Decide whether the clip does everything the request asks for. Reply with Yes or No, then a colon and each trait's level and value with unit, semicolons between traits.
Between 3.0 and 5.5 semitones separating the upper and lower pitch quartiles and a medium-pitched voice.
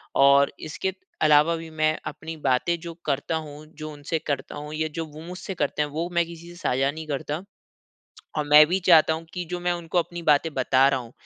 No: narrow, 2.5 semitones; medium, 155 Hz